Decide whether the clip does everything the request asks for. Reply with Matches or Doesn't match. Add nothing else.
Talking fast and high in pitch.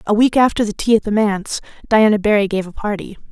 Matches